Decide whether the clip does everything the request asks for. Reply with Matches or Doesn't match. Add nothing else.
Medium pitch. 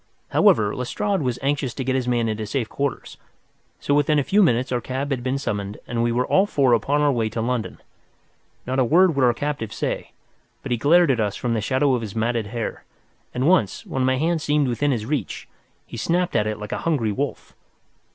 Doesn't match